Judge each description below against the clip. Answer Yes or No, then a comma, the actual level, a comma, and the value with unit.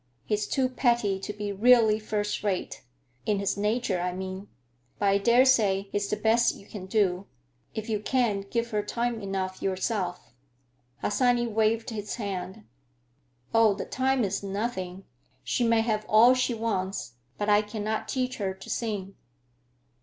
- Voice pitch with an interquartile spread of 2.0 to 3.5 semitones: Yes, average, 2.9 semitones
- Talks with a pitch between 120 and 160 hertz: No, high, 210 Hz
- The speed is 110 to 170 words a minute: Yes, average, 155 wpm